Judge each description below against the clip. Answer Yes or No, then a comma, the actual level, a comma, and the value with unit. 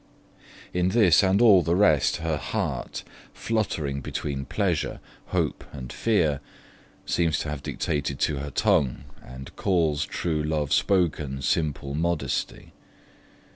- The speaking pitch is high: No, very low, 75 Hz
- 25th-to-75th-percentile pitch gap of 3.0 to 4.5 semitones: Yes, average, 4.1 semitones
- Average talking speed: No, slow, 125 wpm